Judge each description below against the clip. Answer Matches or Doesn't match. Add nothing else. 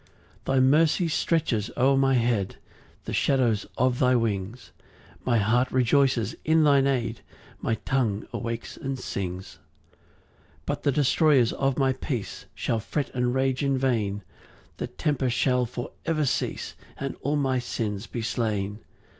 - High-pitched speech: Doesn't match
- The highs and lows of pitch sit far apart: Doesn't match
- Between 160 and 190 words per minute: Doesn't match